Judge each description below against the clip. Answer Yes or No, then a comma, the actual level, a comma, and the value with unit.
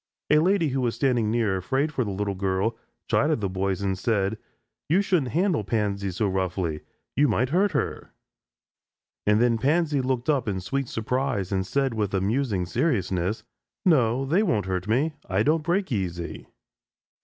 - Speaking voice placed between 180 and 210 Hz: No, low, 115 Hz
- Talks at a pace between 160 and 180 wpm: Yes, average, 165 wpm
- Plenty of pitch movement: Yes, wide, 6.3 semitones